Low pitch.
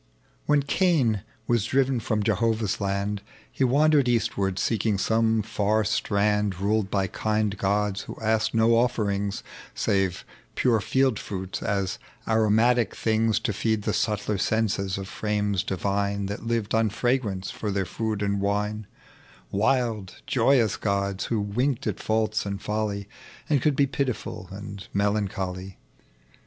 Yes: low, 105 Hz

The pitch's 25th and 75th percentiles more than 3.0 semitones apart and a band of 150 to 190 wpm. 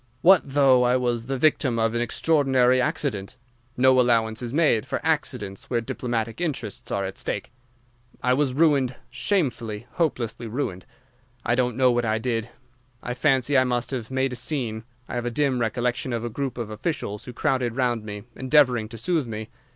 No: average, 2.7 semitones; average, 180 wpm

